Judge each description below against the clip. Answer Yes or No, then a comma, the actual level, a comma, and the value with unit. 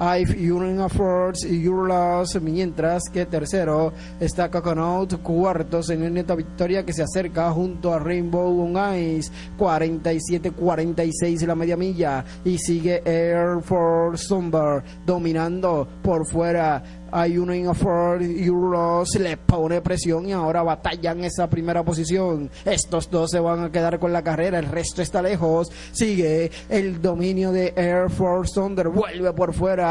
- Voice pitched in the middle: Yes, medium, 175 Hz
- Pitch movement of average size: No, narrow, 1.4 semitones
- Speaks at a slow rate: No, average, 145 wpm